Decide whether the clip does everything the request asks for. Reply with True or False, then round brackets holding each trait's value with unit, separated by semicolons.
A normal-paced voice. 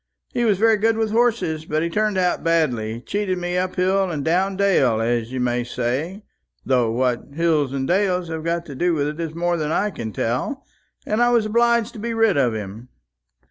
False (215 wpm)